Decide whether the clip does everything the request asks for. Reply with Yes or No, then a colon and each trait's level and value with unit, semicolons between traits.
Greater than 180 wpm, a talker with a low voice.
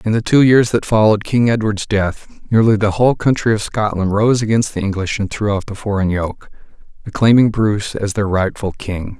Yes: average, 200 wpm; low, 105 Hz